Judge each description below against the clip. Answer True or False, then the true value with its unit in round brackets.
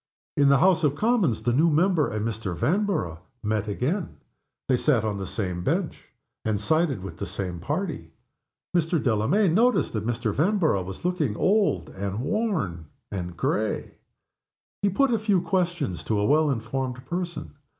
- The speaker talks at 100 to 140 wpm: False (160 wpm)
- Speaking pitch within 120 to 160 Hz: True (135 Hz)